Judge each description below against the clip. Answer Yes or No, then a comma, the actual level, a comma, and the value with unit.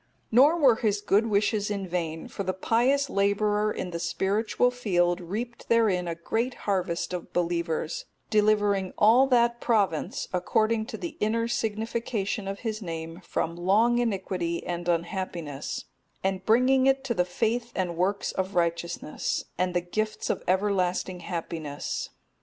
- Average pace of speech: Yes, average, 145 wpm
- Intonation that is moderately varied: Yes, average, 4.3 semitones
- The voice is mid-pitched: No, high, 200 Hz